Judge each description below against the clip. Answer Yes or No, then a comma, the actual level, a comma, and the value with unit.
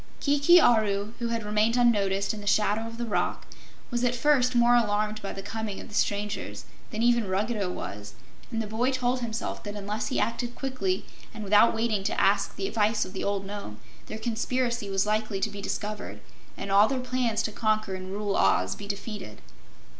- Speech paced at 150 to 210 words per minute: Yes, average, 200 wpm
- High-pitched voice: Yes, high, 215 Hz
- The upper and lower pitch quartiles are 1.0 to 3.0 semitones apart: Yes, average, 2.7 semitones